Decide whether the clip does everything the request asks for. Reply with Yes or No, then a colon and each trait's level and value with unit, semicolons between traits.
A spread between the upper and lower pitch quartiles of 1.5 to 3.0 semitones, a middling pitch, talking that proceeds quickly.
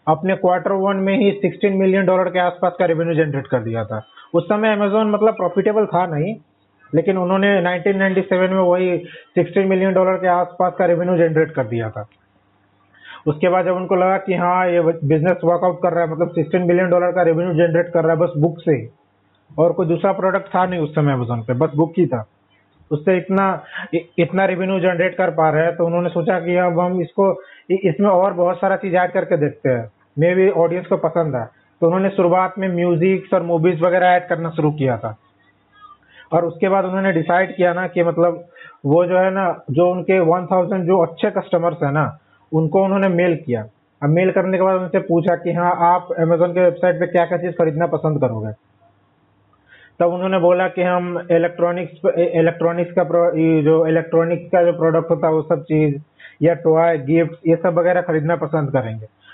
Yes: narrow, 2.4 semitones; medium, 175 Hz; fast, 195 wpm